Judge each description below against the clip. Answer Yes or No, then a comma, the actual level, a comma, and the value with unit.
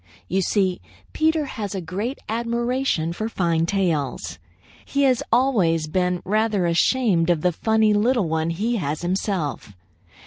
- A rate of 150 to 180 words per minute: No, average, 140 wpm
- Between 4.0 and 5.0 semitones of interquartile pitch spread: No, wide, 5.6 semitones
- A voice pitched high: Yes, high, 195 Hz